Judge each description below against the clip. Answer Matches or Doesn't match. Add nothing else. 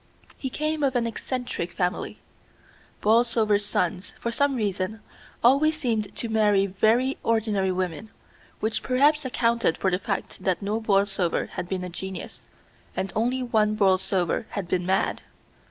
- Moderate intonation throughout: Matches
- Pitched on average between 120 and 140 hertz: Doesn't match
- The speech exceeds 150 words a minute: Doesn't match